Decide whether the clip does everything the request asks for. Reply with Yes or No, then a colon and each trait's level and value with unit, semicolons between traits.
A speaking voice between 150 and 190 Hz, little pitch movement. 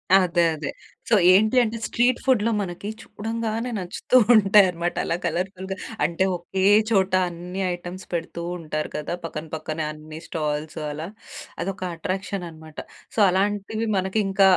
No: medium, 185 Hz; average, 3.5 semitones